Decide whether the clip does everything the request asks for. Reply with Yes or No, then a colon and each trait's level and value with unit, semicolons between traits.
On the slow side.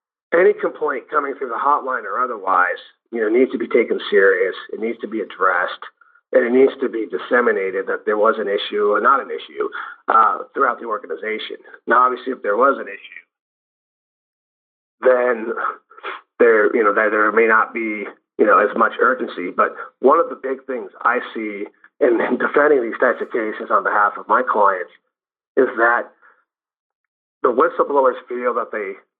No: average, 175 wpm